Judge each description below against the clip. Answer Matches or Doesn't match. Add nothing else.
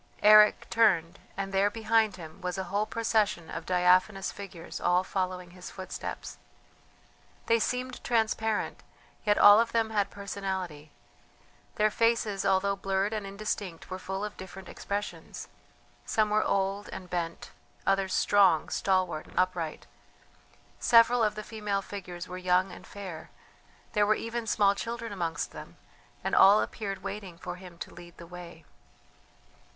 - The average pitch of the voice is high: Matches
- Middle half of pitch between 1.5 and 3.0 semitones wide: Matches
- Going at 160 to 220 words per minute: Doesn't match